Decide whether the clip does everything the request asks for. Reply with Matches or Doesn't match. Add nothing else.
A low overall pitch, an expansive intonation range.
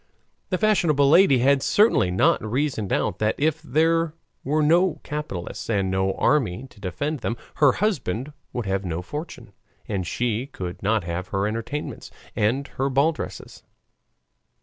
Matches